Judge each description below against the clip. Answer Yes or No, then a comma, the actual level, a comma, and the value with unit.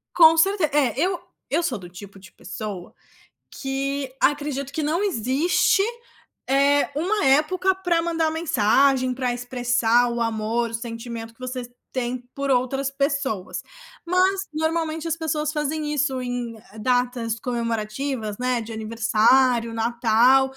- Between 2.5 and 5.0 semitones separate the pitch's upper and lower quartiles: Yes, average, 4.5 semitones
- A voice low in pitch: No, very high, 260 Hz